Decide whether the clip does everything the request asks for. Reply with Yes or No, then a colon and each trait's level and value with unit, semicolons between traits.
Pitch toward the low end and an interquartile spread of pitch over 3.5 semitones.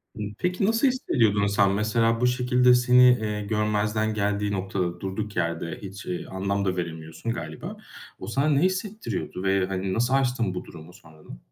Yes: low, 105 Hz; average, 4.7 semitones